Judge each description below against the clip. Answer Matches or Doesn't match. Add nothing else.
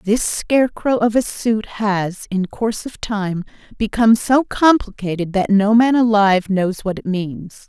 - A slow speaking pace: Doesn't match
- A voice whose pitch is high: Matches